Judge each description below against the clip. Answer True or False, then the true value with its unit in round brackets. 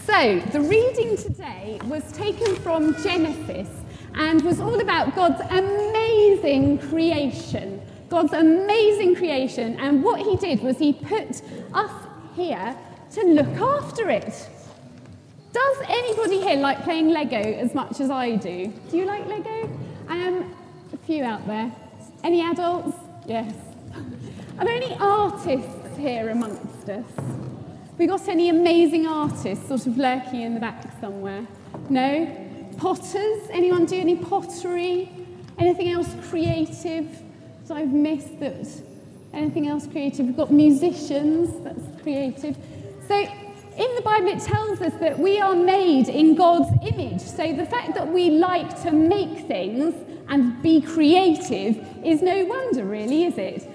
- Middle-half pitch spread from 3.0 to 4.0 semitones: False (4.5 semitones)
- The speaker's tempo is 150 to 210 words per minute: False (140 wpm)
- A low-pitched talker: False (330 Hz)